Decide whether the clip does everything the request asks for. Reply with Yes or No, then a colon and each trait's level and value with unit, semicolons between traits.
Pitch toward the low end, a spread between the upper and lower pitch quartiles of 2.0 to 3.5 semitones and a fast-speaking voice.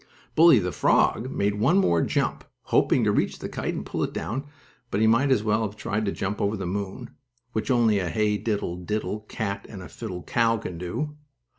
Yes: low, 105 Hz; average, 2.8 semitones; fast, 210 wpm